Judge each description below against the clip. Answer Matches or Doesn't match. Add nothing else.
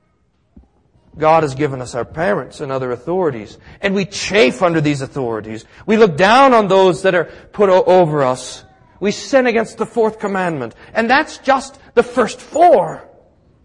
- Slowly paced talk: Doesn't match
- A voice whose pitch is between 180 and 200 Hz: Matches